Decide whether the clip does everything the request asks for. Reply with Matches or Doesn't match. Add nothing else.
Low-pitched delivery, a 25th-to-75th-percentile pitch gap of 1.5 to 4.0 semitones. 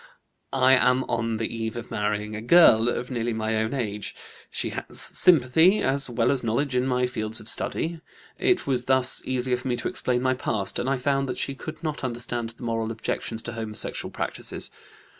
Matches